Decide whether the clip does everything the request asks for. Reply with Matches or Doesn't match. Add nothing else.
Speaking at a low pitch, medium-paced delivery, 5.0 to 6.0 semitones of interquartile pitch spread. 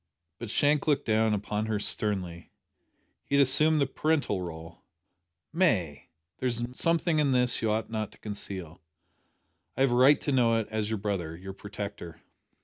Matches